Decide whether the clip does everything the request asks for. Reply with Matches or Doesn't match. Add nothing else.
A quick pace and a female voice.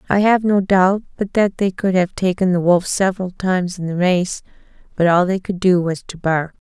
Matches